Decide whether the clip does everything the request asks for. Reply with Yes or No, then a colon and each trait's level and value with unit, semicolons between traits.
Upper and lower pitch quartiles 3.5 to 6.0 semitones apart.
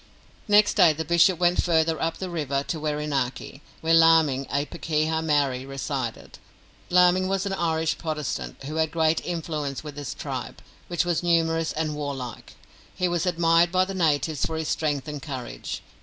No: average, 2.7 semitones